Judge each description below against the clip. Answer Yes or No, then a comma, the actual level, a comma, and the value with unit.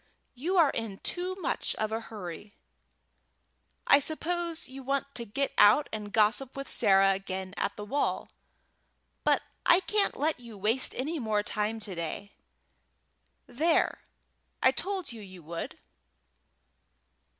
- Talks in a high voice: Yes, high, 230 Hz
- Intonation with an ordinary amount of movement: No, wide, 6.3 semitones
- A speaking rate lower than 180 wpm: Yes, average, 140 wpm